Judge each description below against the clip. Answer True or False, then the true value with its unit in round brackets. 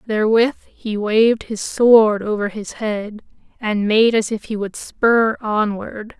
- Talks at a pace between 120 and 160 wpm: True (155 wpm)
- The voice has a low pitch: False (215 Hz)